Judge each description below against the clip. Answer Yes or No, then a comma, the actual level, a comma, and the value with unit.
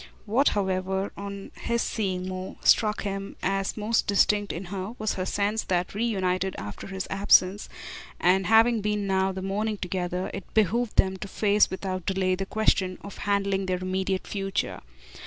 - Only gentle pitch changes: Yes, narrow, 1.9 semitones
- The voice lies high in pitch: Yes, high, 195 Hz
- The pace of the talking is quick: No, average, 170 wpm